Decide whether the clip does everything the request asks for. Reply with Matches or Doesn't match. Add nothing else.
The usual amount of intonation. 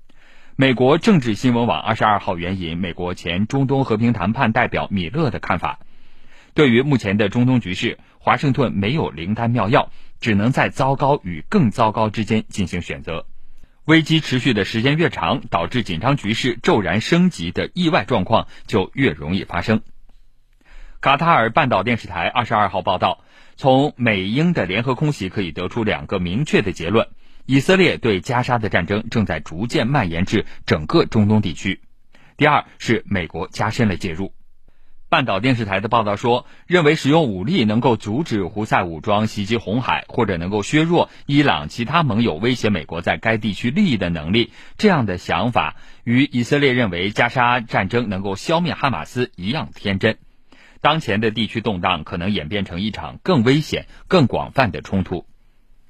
Matches